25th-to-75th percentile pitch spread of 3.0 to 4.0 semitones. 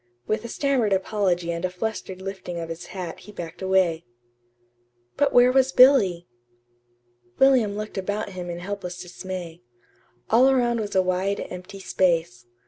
Yes: average, 3.6 semitones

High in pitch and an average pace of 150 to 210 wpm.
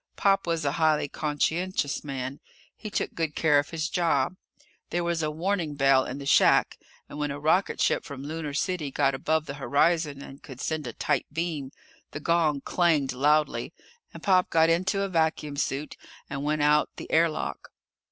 No: medium, 150 Hz; average, 180 wpm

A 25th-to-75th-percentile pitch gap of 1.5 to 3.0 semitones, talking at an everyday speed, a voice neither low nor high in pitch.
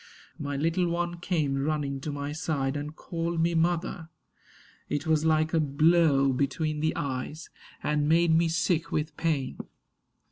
Yes: narrow, 2.4 semitones; average, 150 wpm; medium, 155 Hz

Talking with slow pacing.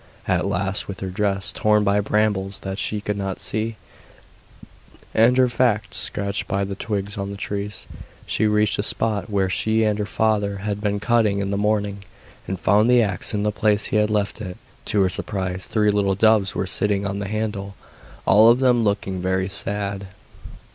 No: average, 190 wpm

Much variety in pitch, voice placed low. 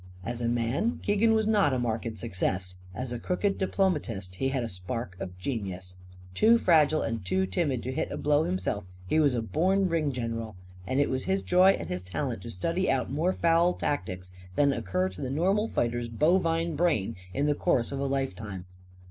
Yes: wide, 8.3 semitones; low, 130 Hz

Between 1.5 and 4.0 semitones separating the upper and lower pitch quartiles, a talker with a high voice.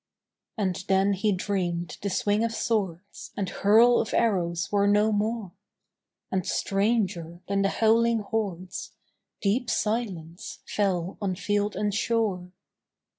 Yes: average, 2.9 semitones; high, 200 Hz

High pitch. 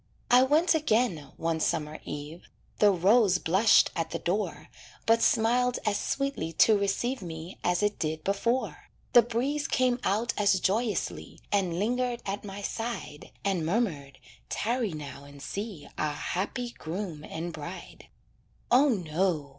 Yes: high, 200 Hz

